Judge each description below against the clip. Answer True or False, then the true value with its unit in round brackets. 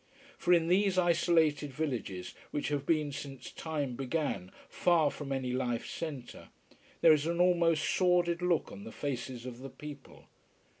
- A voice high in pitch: False (150 Hz)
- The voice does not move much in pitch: False (4.4 semitones)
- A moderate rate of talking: True (155 wpm)